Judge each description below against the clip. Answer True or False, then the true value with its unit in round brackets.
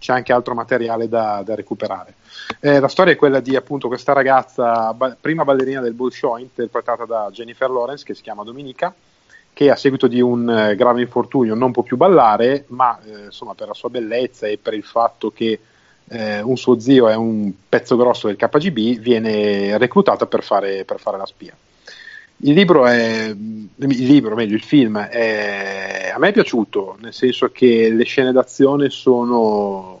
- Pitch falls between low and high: False (120 Hz)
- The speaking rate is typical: False (180 wpm)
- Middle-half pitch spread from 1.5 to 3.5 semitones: True (3.2 semitones)